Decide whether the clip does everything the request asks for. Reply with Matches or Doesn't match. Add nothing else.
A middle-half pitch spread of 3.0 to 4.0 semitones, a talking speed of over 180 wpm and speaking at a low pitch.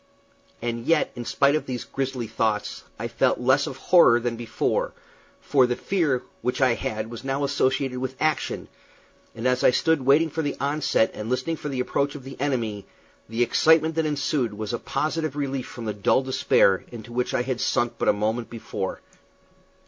Matches